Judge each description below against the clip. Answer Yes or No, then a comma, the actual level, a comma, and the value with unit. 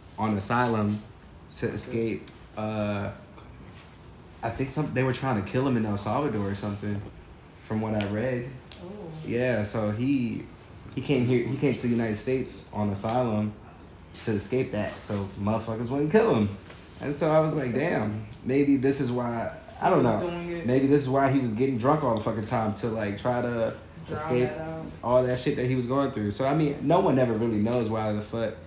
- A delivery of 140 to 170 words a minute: No, average, 195 wpm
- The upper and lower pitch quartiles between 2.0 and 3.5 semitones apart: No, average, 3.9 semitones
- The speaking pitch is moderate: No, low, 115 Hz